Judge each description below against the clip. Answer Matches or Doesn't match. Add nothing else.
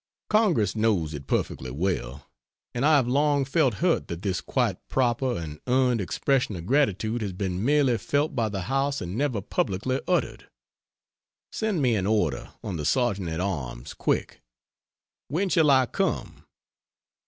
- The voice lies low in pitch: Matches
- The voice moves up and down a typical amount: Doesn't match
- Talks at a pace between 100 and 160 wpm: Matches